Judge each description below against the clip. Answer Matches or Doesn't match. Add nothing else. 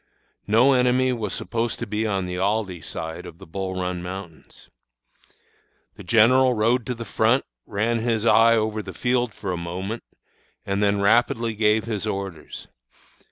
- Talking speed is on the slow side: Doesn't match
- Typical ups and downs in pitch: Matches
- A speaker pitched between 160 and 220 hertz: Doesn't match